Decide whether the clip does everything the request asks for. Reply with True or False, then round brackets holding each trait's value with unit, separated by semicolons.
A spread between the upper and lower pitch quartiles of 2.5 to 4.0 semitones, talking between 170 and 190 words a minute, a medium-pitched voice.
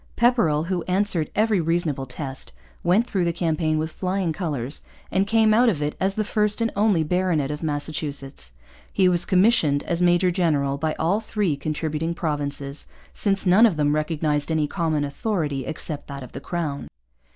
False (4.4 semitones; 175 wpm; 165 Hz)